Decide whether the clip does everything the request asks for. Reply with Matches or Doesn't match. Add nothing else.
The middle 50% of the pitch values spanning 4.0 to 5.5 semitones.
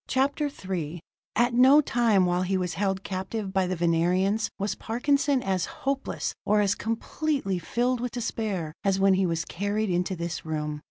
Matches